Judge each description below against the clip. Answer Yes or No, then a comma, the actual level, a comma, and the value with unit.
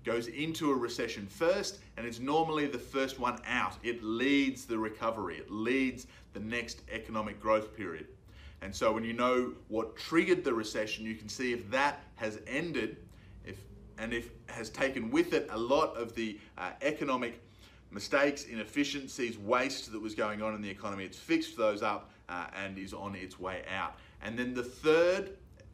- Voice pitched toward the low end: Yes, low, 115 Hz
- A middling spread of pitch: Yes, average, 3.7 semitones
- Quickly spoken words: No, average, 180 wpm